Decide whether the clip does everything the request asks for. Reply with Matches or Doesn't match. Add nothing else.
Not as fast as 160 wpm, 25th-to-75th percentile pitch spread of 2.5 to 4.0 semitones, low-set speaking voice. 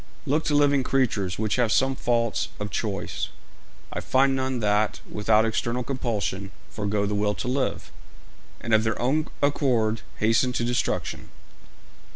Matches